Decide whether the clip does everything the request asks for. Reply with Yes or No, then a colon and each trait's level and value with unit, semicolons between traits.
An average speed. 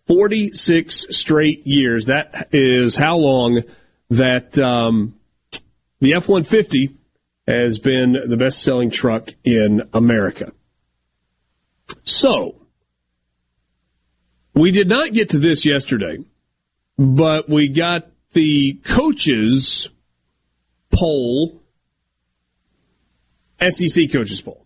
No: slow, 90 wpm